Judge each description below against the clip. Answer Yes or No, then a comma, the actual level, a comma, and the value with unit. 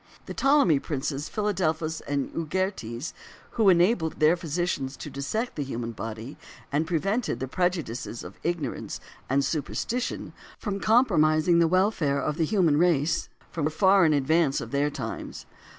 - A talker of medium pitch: Yes, medium, 160 Hz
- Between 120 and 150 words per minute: Yes, average, 145 wpm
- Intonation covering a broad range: No, average, 4.7 semitones